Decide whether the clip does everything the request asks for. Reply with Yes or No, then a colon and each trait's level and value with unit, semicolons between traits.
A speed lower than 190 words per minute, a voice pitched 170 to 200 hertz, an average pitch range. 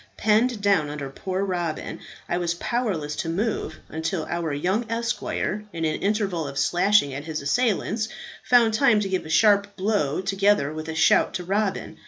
Yes: average, 175 wpm; high, 190 Hz; average, 4.8 semitones